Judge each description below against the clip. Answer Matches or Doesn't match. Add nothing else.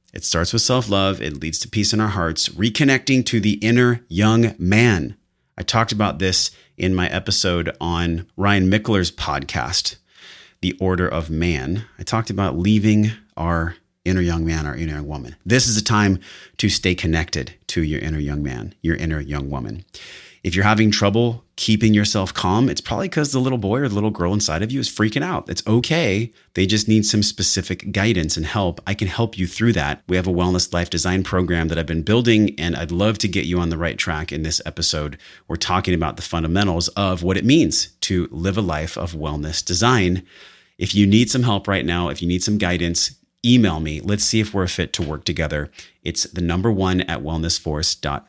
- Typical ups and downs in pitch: Matches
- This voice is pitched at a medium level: Doesn't match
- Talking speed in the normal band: Doesn't match